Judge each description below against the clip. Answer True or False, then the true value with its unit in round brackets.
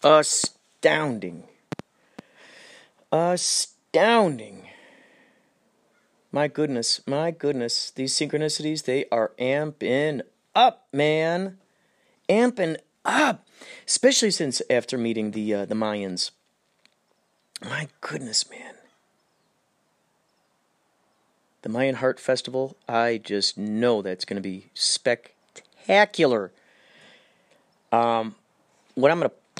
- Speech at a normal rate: False (80 wpm)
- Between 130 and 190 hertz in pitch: True (135 Hz)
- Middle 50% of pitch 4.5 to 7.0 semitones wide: True (5.3 semitones)